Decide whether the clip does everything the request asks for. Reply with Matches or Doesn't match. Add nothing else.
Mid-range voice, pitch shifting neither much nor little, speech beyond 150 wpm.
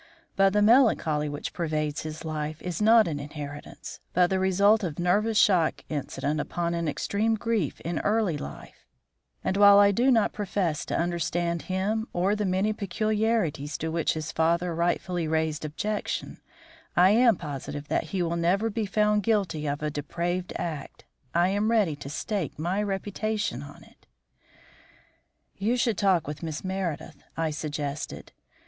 Matches